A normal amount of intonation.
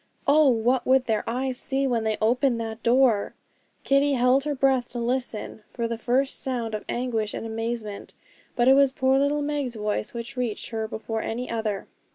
Yes: average, 3.0 semitones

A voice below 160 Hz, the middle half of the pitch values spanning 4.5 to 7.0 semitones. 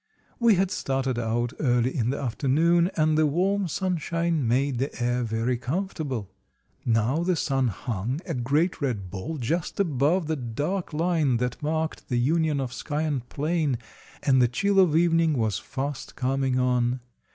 Yes: medium, 140 Hz; average, 4.8 semitones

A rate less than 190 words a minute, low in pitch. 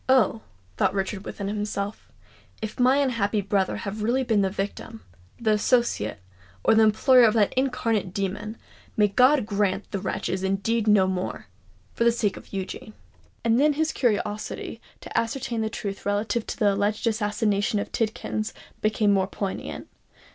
No: average, 160 wpm; high, 210 Hz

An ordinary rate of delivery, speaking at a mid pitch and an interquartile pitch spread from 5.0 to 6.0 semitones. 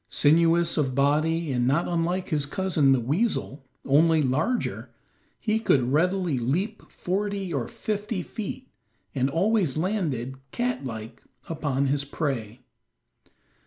No: slow, 125 wpm; medium, 160 Hz; wide, 5.6 semitones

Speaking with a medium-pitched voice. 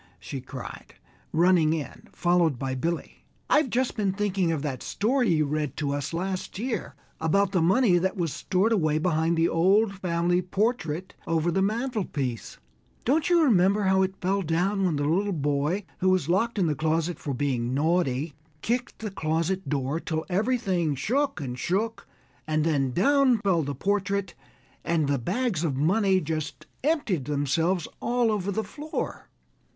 Yes: medium, 175 Hz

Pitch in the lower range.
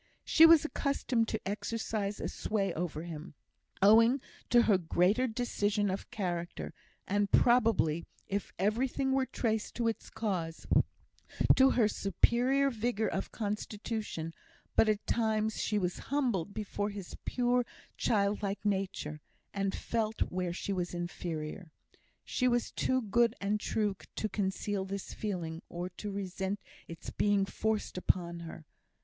No: high, 205 Hz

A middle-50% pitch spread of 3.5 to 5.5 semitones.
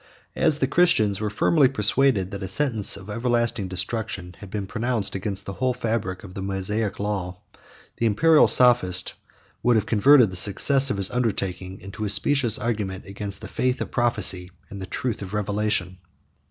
Yes: average, 3.9 semitones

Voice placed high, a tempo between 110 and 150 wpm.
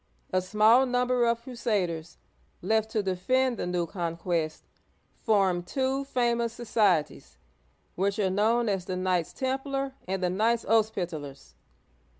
Yes: high, 210 Hz; slow, 135 wpm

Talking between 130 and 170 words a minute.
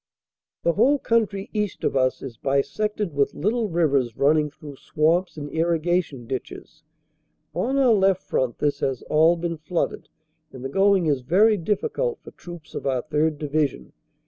Yes: average, 160 wpm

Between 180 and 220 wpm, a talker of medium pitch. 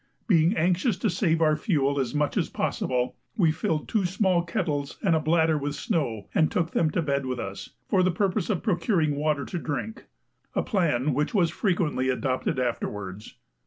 Yes: average, 185 wpm; medium, 155 Hz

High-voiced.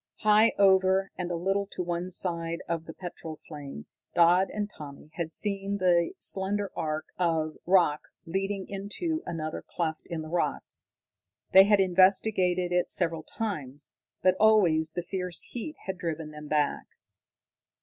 No: medium, 180 Hz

